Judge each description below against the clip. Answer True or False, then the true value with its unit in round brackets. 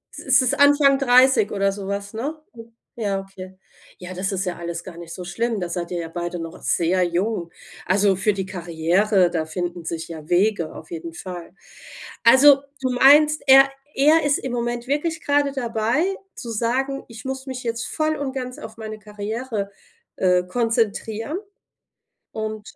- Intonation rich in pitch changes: True (6.3 semitones)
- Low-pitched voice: False (215 Hz)